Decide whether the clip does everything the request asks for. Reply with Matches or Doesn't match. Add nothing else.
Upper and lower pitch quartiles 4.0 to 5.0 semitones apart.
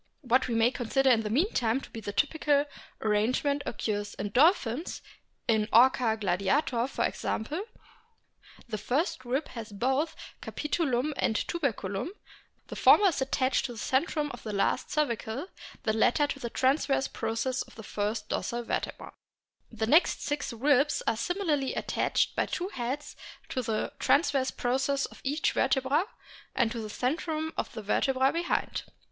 Matches